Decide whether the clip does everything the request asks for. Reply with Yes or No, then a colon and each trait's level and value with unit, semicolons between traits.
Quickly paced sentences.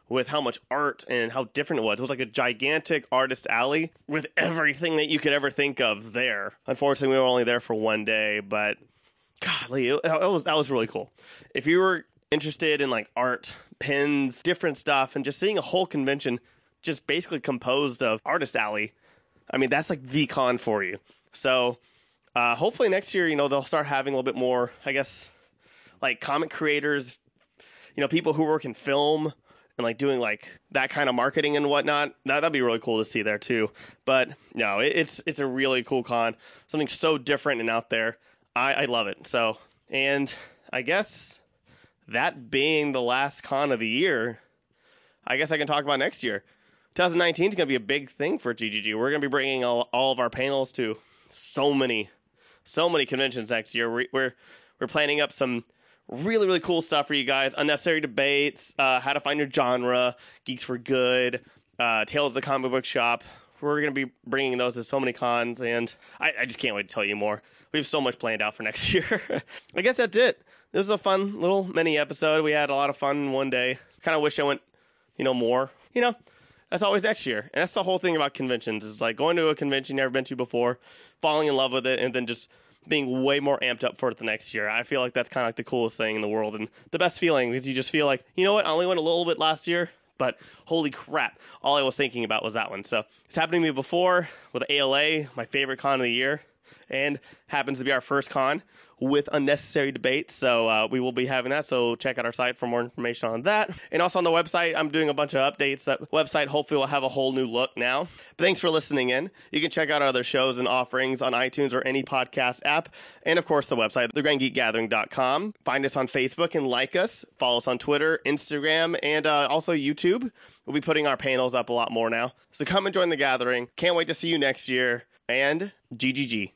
Yes: fast, 230 wpm